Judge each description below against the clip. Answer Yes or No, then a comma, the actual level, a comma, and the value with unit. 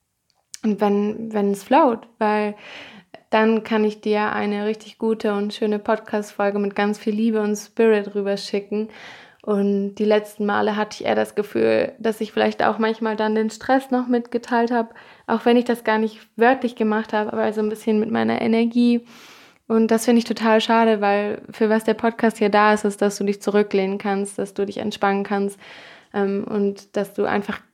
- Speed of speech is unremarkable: No, fast, 195 wpm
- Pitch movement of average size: No, narrow, 1.7 semitones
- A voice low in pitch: No, high, 215 Hz